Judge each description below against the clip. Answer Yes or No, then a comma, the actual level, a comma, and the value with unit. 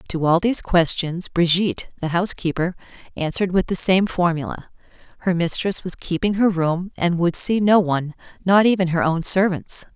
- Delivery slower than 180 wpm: Yes, average, 170 wpm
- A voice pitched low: No, medium, 180 Hz